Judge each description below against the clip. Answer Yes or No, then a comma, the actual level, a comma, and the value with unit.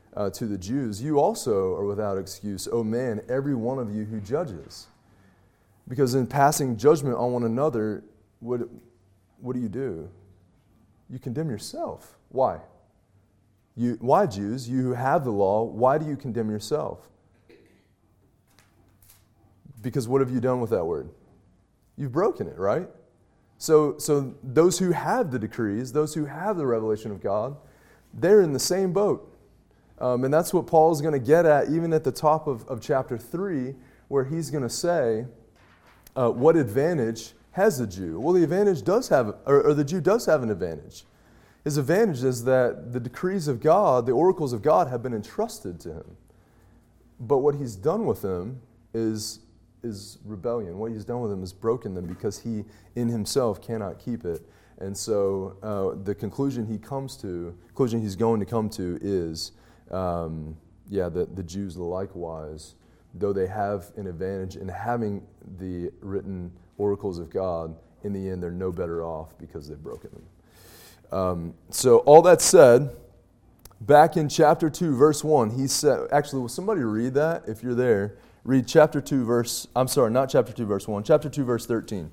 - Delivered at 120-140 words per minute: No, average, 175 wpm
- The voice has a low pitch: Yes, low, 115 Hz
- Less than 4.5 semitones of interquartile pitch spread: No, wide, 5.4 semitones